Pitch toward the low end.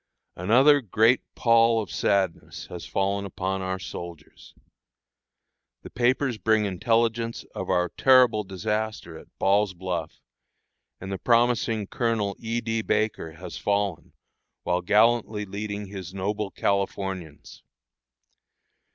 Yes: low, 100 Hz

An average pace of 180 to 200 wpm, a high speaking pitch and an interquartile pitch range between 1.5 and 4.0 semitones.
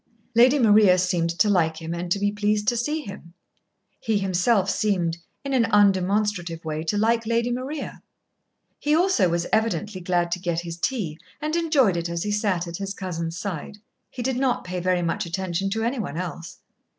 No: average, 190 wpm; high, 195 Hz; average, 4.7 semitones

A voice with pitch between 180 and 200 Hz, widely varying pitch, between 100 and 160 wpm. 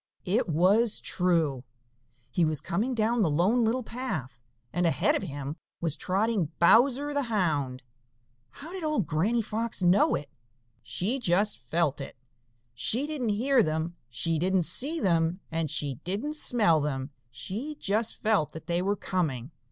Yes: medium, 185 Hz; wide, 6.7 semitones; average, 155 wpm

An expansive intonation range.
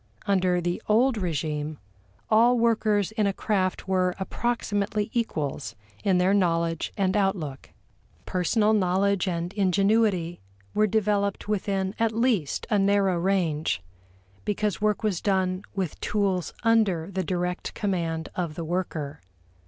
No: average, 3.2 semitones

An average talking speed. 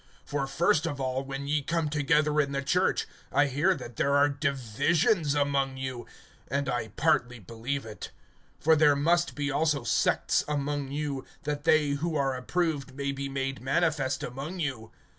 Yes: average, 170 wpm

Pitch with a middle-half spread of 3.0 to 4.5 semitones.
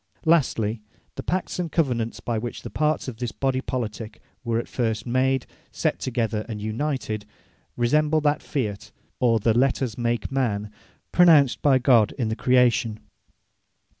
Yes: average, 3.4 semitones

